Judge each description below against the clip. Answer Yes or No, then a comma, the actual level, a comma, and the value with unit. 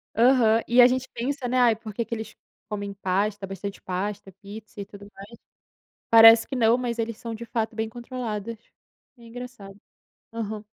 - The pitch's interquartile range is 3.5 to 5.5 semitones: No, average, 2.7 semitones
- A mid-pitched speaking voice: No, high, 225 Hz